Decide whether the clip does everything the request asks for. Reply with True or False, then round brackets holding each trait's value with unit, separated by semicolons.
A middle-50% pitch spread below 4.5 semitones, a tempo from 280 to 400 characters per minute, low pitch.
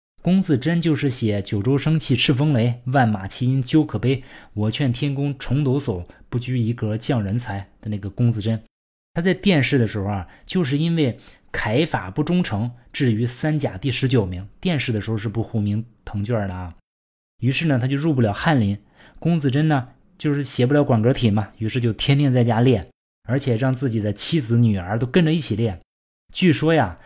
False (4.9 semitones; 285 characters per minute; 125 Hz)